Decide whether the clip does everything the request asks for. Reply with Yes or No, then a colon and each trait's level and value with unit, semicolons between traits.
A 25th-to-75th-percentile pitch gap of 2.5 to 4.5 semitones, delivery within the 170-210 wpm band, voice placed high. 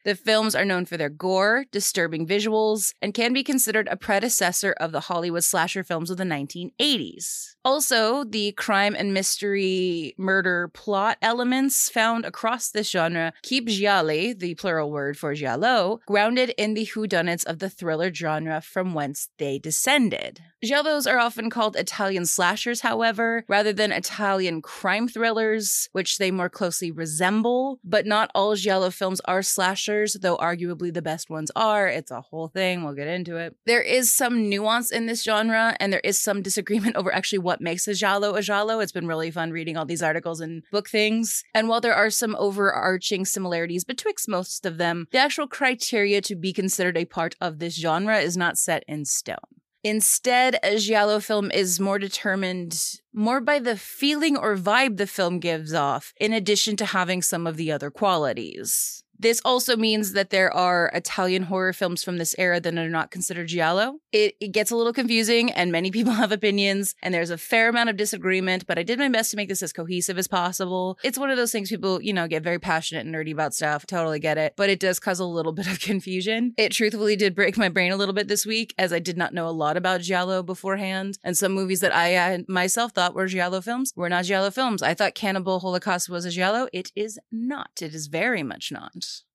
Yes: average, 3.8 semitones; average, 200 wpm; high, 195 Hz